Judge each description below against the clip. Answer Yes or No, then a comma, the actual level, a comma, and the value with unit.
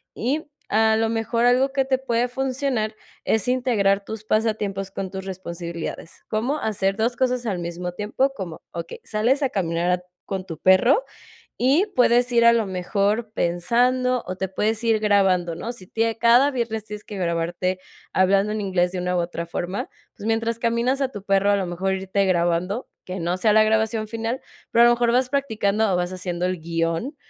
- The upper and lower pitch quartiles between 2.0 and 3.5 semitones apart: No, average, 4.2 semitones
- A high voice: Yes, high, 215 Hz